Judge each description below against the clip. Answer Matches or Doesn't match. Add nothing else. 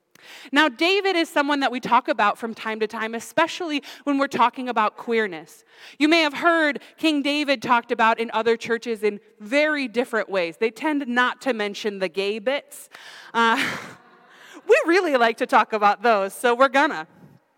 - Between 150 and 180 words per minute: Matches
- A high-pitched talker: Matches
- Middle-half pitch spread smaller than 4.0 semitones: Doesn't match